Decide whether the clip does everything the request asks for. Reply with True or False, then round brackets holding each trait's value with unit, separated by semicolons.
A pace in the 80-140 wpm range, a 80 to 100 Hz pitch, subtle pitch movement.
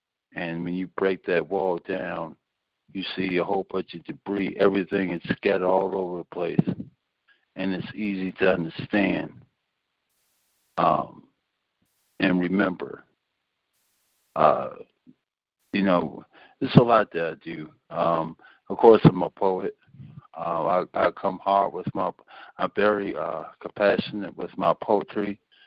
True (135 wpm; 95 Hz; 2.0 semitones)